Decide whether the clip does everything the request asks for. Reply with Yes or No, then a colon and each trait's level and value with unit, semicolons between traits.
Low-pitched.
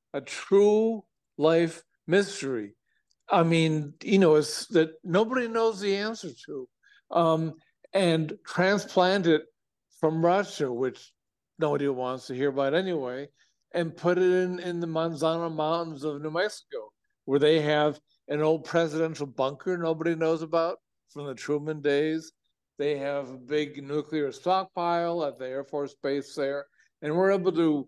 No: medium, 160 Hz